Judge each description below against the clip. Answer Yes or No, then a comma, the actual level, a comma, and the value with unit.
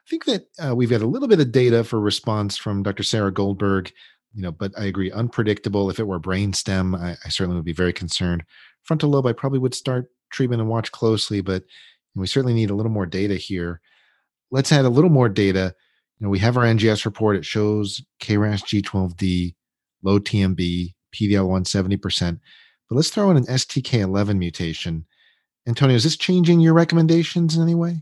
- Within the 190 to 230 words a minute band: Yes, average, 195 wpm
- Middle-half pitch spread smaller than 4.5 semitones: No, average, 5.1 semitones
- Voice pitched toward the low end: Yes, low, 105 Hz